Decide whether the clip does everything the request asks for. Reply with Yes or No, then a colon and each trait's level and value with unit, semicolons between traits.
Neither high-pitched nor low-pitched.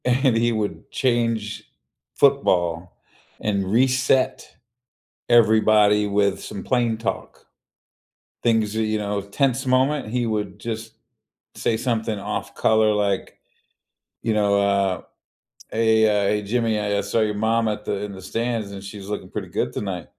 No: low, 110 Hz